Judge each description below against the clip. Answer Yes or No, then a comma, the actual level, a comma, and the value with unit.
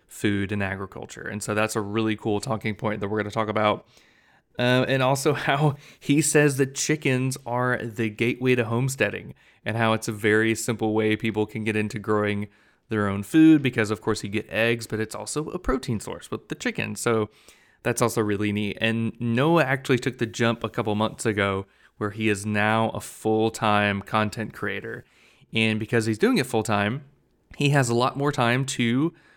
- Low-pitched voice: Yes, low, 110 Hz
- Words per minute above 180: Yes, average, 200 wpm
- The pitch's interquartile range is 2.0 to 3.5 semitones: Yes, average, 2.9 semitones